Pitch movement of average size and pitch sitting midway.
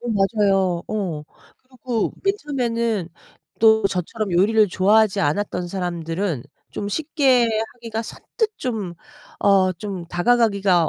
No: average, 4.2 semitones; high, 205 Hz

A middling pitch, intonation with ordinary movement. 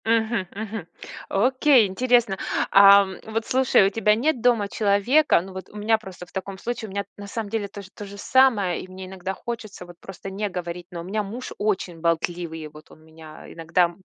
No: high, 200 Hz; average, 3.7 semitones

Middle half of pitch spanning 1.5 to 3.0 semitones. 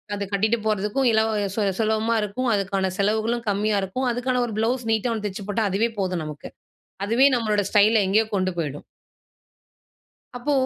Yes: average, 2.7 semitones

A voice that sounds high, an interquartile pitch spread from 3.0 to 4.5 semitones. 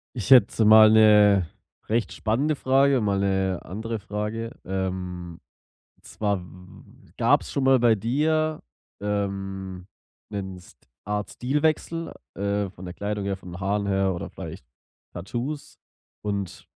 No: low, 105 Hz; average, 3.3 semitones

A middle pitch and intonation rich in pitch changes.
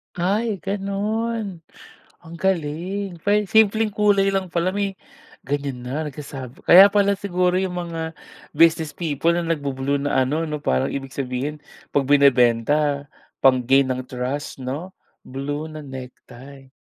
Yes: medium, 155 Hz; wide, 5.9 semitones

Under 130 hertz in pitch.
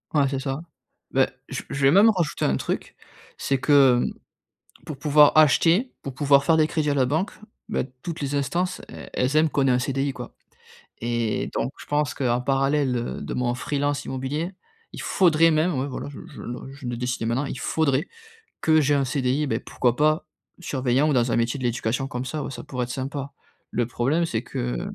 No: medium, 140 Hz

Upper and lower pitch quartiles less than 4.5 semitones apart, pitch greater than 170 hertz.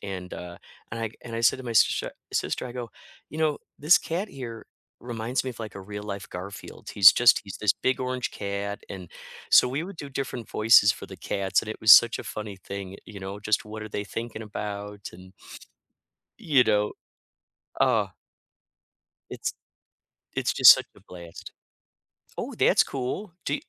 No: average, 3.9 semitones; low, 110 Hz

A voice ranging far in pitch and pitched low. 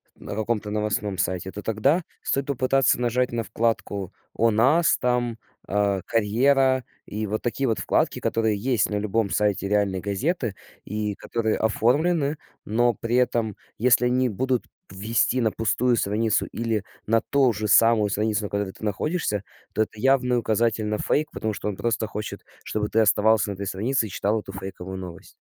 No: average, 3.0 semitones; low, 110 Hz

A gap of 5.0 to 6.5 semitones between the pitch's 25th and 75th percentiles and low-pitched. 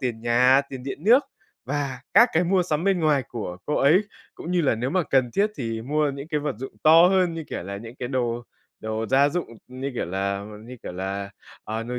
Yes: average, 5.3 semitones; low, 130 Hz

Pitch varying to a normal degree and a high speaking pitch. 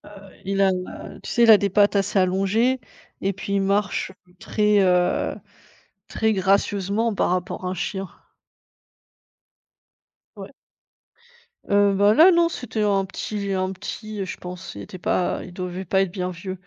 No: narrow, 2.0 semitones; high, 195 Hz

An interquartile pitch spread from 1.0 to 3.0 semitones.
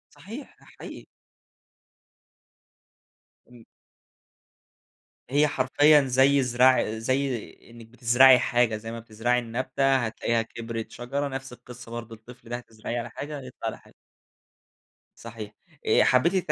Yes: narrow, 2.5 semitones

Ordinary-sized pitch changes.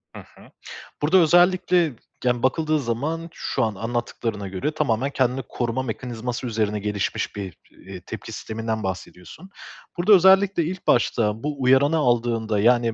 No: wide, 5.8 semitones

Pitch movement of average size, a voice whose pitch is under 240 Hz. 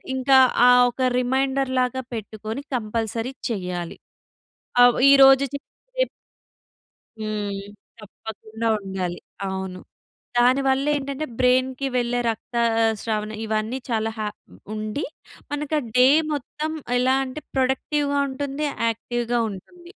No: average, 3.7 semitones; high, 245 Hz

